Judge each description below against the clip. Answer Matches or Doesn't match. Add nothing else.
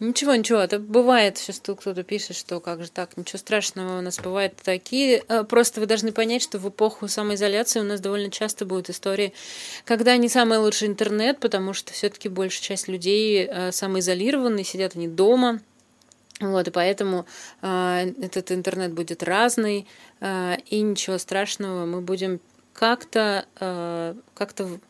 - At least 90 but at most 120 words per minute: Doesn't match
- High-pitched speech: Matches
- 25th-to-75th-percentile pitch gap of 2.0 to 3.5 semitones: Matches